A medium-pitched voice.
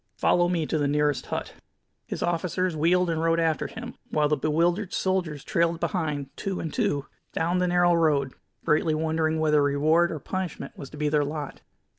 Yes: medium, 160 Hz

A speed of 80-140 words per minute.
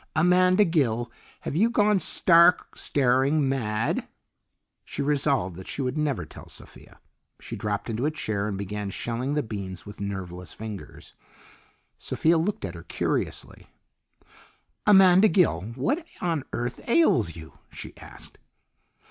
Yes: slow, 135 wpm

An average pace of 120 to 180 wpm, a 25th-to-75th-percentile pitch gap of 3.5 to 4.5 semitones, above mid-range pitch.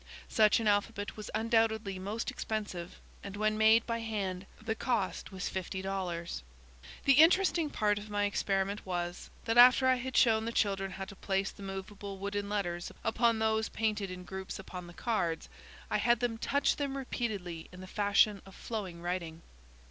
No: average, 175 wpm; average, 2.9 semitones; high, 205 Hz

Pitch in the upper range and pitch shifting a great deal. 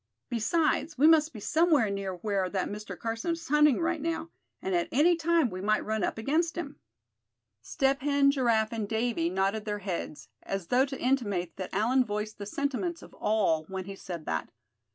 Yes: high, 225 Hz; wide, 6.8 semitones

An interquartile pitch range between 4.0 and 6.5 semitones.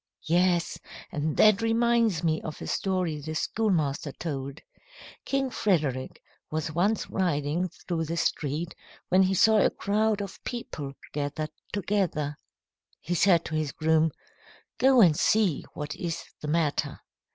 Yes: average, 4.8 semitones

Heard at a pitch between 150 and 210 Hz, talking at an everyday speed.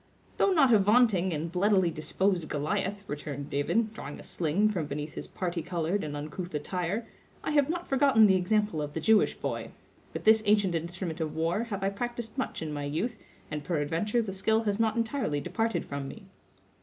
Yes: high, 190 Hz; average, 195 wpm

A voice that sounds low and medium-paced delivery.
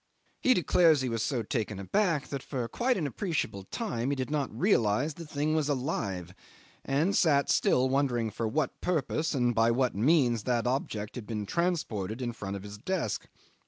Yes: low, 130 Hz; average, 185 wpm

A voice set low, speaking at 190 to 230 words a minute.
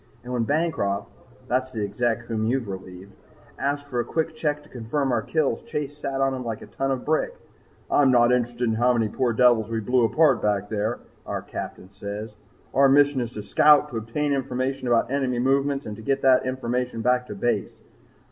Yes: low, 125 Hz; average, 200 wpm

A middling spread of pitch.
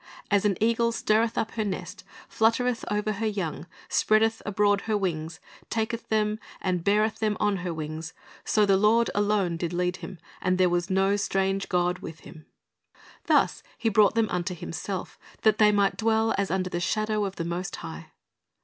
Yes: average, 3.3 semitones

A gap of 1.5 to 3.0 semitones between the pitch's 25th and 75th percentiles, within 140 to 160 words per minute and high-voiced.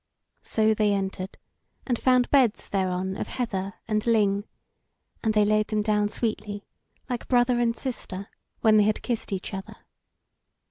Yes: average, 2.7 semitones; average, 150 wpm; high, 215 Hz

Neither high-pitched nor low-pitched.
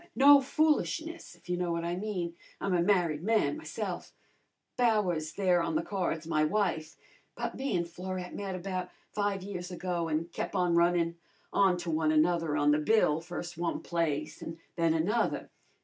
Yes: medium, 175 Hz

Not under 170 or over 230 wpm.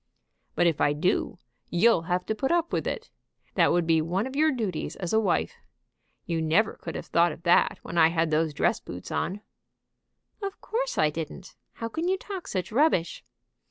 Yes: average, 195 wpm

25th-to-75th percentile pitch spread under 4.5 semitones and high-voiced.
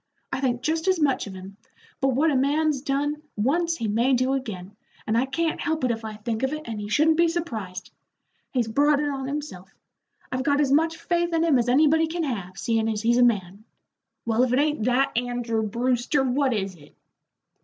No: average, 4.9 semitones; very high, 255 Hz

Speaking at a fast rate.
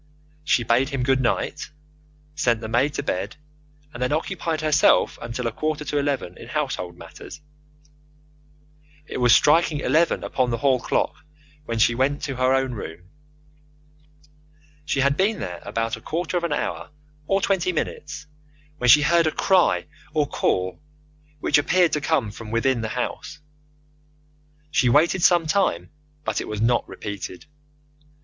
No: average, 155 wpm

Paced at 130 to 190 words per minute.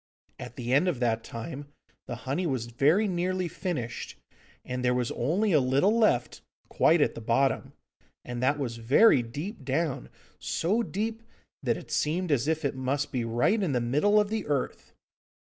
Yes: average, 175 wpm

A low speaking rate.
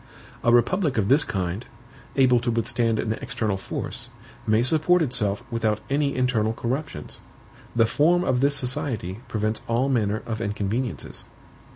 No: average, 145 wpm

